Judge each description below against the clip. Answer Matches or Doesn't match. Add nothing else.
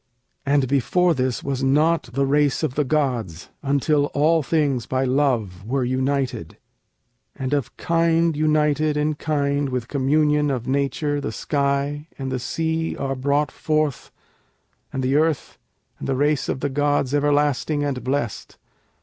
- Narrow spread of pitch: Matches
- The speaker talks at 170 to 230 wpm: Doesn't match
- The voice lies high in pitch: Doesn't match